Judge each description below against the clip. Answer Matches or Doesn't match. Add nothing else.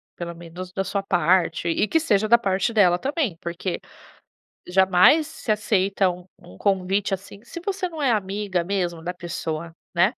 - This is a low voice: Doesn't match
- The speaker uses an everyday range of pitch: Matches